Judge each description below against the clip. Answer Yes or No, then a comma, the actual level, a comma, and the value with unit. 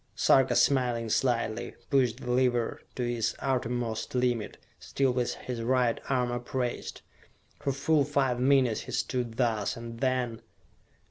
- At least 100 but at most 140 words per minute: Yes, slow, 135 wpm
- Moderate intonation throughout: No, narrow, 1.8 semitones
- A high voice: No, low, 125 Hz